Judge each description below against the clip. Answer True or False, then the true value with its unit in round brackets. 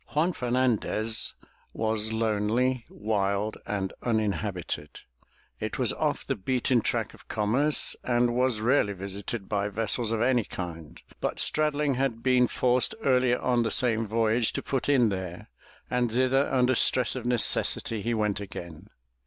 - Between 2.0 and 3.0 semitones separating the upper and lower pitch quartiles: False (3.4 semitones)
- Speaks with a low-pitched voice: True (115 Hz)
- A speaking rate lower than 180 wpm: True (145 wpm)